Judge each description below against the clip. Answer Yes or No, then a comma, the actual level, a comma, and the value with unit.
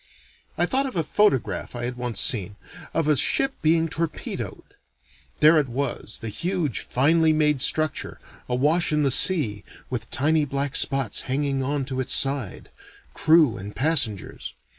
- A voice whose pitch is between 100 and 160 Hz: Yes, medium, 140 Hz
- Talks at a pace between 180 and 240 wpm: No, average, 155 wpm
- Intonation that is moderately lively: Yes, average, 4.2 semitones